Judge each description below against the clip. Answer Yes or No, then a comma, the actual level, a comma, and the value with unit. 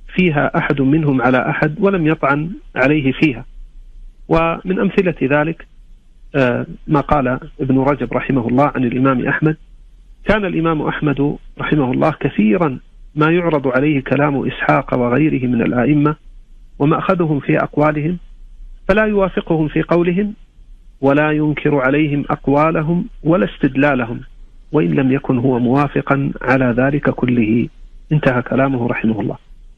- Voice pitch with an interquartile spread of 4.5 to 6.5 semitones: No, average, 3.2 semitones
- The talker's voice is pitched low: No, medium, 145 Hz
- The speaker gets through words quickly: No, average, 120 wpm